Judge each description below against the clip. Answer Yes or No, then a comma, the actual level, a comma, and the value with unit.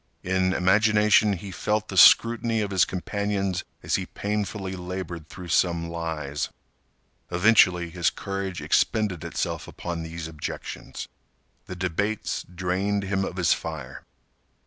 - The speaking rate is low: Yes, slow, 125 wpm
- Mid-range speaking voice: No, very low, 95 Hz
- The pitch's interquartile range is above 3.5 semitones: No, average, 3.0 semitones